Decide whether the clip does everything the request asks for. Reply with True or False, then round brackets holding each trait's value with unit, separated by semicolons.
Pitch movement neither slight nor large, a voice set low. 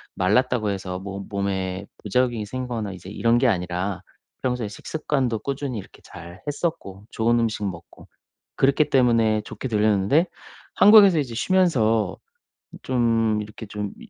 True (4.3 semitones; 110 Hz)